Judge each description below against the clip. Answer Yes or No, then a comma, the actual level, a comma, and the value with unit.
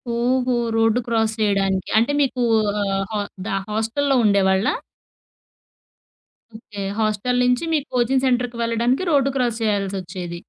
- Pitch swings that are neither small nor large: Yes, average, 3.7 semitones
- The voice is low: No, high, 225 Hz